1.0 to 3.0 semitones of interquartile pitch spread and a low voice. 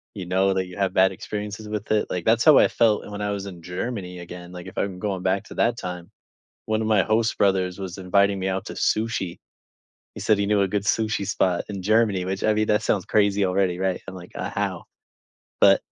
Yes: narrow, 2.4 semitones; low, 100 Hz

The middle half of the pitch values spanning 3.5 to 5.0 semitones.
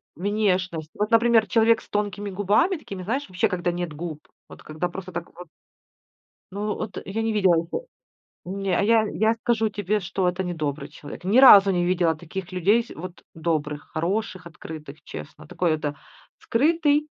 Yes: average, 4.2 semitones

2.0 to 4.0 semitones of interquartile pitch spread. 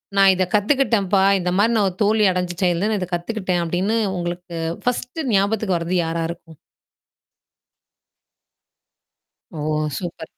Yes: average, 3.3 semitones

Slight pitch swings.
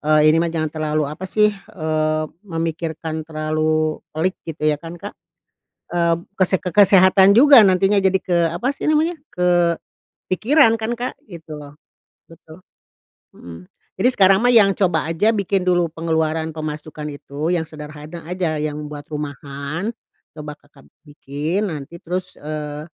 No: average, 3.6 semitones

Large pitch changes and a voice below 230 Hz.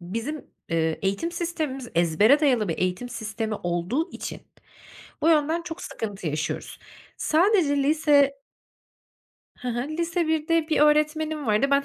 No: wide, 6.8 semitones; very high, 280 Hz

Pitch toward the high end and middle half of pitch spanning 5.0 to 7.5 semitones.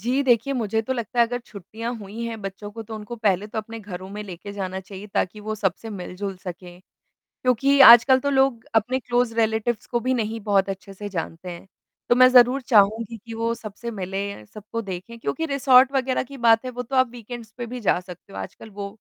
No: high, 225 Hz; average, 3.5 semitones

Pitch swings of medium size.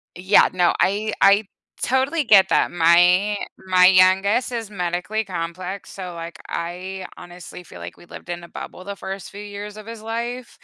Yes: average, 3.0 semitones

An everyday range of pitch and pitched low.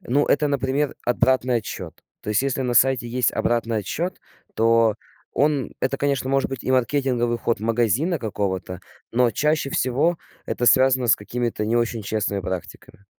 Yes: average, 3.0 semitones; low, 120 Hz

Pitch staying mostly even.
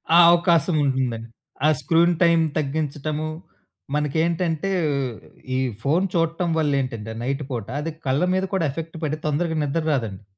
No: average, 3.5 semitones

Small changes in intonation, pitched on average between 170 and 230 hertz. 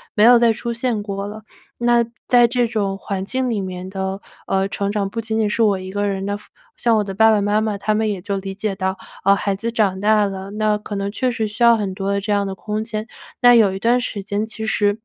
Yes: narrow, 2.1 semitones; high, 210 Hz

